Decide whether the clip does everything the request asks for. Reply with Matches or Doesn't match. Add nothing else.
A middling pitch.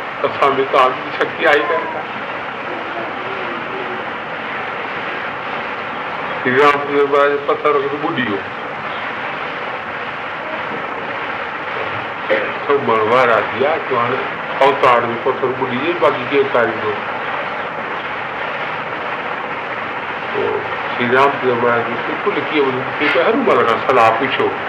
Matches